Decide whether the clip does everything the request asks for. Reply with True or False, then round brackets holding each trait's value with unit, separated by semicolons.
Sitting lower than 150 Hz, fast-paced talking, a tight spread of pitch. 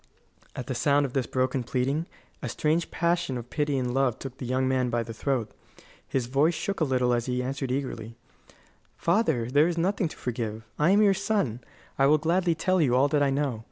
False (135 Hz; 215 wpm; 4.3 semitones)